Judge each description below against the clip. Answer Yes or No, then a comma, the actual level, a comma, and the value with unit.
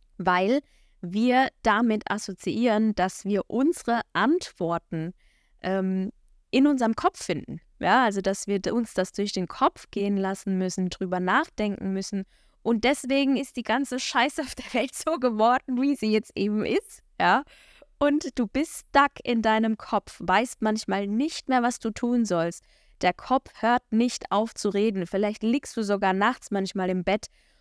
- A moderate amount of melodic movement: Yes, average, 4.7 semitones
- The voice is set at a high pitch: Yes, high, 220 Hz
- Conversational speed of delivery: Yes, average, 165 wpm